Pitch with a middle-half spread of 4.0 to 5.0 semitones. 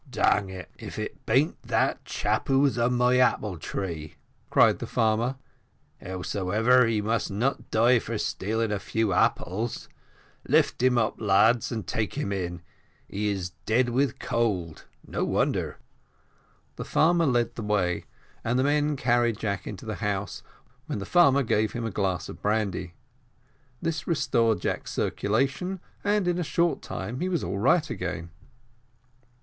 Yes: average, 4.4 semitones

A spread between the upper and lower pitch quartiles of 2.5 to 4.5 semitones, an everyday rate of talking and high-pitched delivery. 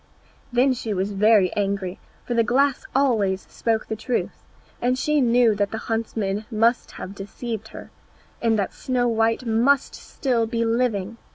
Yes: average, 2.9 semitones; average, 160 wpm; high, 225 Hz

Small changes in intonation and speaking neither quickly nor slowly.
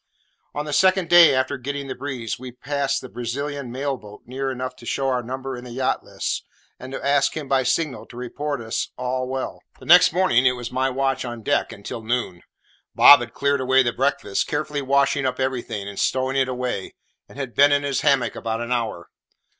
No: narrow, 2.3 semitones; fast, 210 wpm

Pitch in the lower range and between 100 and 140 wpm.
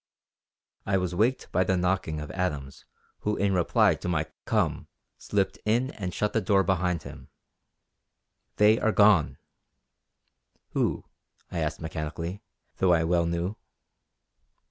Yes: very low, 90 Hz; slow, 135 wpm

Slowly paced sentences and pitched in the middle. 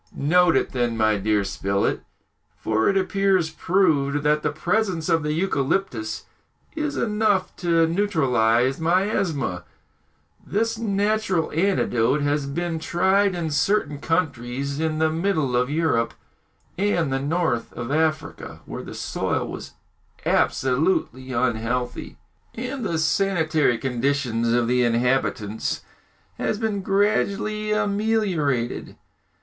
Yes: slow, 115 wpm; medium, 160 Hz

